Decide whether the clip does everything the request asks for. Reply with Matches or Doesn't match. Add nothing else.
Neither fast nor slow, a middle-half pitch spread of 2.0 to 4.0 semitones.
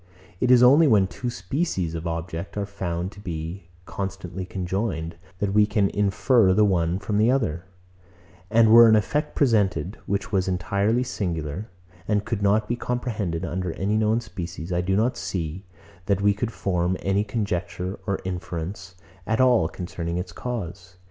Matches